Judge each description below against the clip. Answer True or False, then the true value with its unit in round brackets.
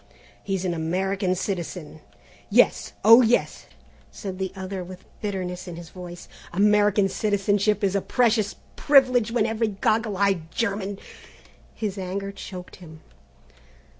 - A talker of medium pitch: False (195 Hz)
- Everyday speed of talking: False (120 wpm)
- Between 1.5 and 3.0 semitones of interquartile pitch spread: True (2.4 semitones)